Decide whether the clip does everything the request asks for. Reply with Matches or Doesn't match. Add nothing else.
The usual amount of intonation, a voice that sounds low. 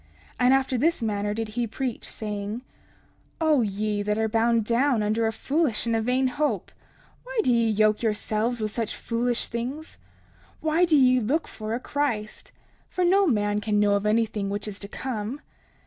Doesn't match